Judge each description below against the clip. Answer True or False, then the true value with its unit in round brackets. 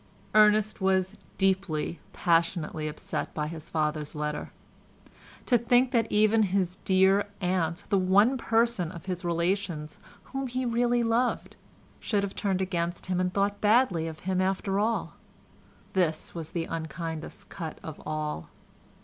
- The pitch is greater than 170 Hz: True (185 Hz)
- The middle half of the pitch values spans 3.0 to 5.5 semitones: True (4.2 semitones)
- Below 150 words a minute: True (140 wpm)